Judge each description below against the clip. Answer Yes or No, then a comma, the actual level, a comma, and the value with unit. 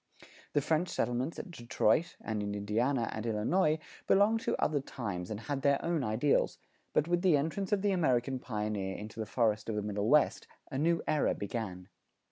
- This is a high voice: No, low, 125 Hz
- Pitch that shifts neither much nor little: No, wide, 6.6 semitones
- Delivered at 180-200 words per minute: Yes, average, 185 wpm